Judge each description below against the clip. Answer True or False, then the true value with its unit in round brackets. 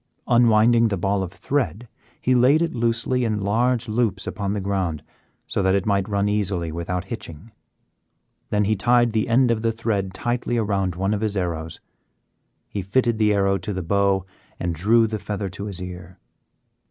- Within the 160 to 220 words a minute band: True (180 wpm)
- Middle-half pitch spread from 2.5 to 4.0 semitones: True (3.4 semitones)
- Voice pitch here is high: False (100 Hz)